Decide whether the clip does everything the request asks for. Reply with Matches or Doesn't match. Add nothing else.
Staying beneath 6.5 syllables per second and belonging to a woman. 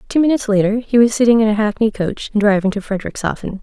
Doesn't match